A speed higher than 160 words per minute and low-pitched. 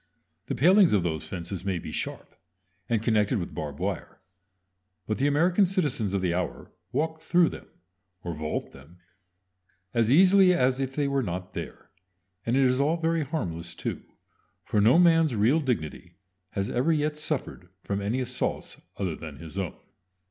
Yes: average, 170 wpm; low, 120 Hz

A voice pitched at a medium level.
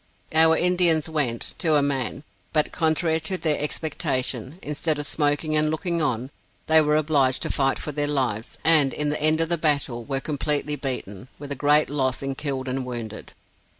Yes: medium, 150 Hz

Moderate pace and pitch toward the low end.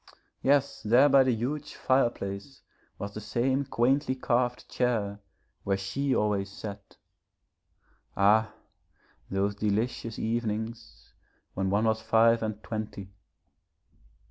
No: slow, 110 wpm; low, 110 Hz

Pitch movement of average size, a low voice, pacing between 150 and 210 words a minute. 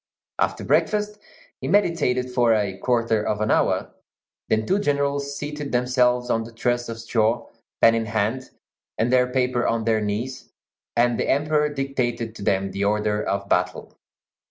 Yes: average, 3.6 semitones; low, 120 Hz; average, 160 wpm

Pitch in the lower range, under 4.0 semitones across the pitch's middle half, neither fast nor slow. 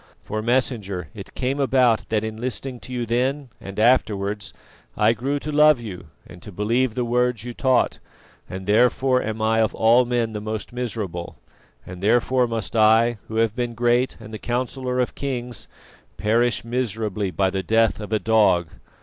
Yes: low, 115 Hz; average, 2.7 semitones; average, 175 wpm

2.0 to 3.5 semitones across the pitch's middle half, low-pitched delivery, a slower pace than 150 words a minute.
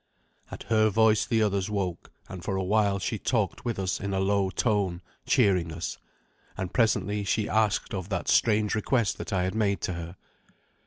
No: narrow, 2.5 semitones; low, 100 Hz; average, 190 wpm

